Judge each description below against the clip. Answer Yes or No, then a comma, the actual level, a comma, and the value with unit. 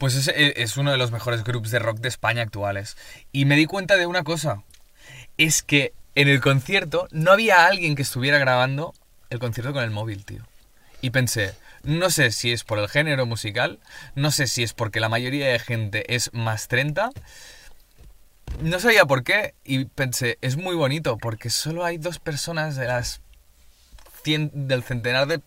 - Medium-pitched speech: No, low, 130 Hz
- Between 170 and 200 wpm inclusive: Yes, average, 185 wpm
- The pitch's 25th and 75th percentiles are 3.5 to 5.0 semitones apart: Yes, average, 4.3 semitones